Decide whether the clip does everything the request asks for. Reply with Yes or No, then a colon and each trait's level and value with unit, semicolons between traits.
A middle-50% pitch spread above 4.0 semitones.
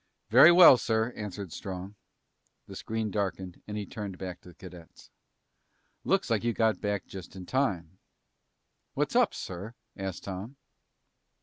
No: average, 3.3 semitones